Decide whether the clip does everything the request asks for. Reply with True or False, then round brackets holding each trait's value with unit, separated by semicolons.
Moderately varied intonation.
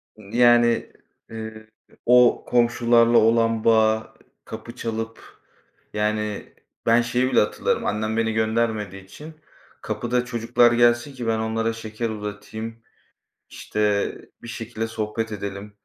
False (1.5 semitones)